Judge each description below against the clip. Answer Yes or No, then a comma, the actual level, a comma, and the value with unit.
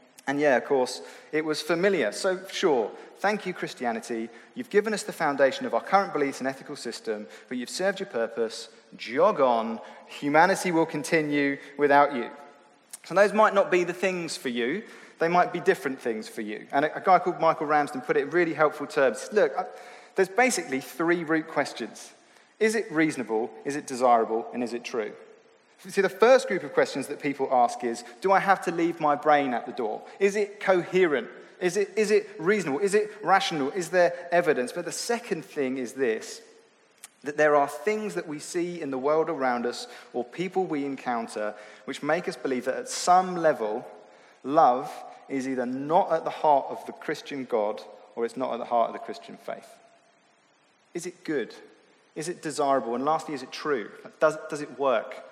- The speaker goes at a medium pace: Yes, average, 195 wpm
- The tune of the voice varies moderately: No, wide, 6.3 semitones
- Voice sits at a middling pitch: Yes, medium, 155 Hz